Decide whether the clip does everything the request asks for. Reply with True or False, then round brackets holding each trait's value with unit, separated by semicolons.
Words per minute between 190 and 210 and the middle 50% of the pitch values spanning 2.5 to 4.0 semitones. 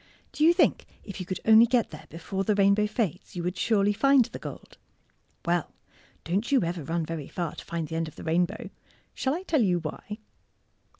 False (205 wpm; 4.7 semitones)